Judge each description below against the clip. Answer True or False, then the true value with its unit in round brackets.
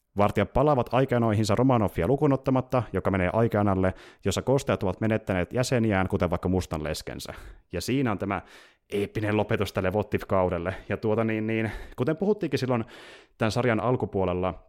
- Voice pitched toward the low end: True (105 Hz)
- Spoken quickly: False (145 wpm)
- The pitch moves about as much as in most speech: True (4.5 semitones)